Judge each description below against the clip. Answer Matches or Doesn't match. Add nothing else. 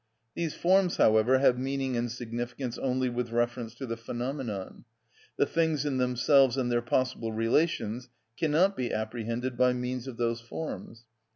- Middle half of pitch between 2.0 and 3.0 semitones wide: Matches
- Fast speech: Doesn't match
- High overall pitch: Doesn't match